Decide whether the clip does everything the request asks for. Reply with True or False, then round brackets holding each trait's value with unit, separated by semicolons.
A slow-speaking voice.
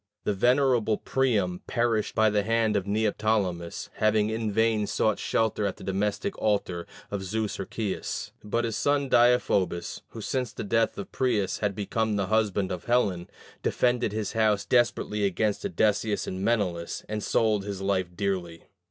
False (160 wpm)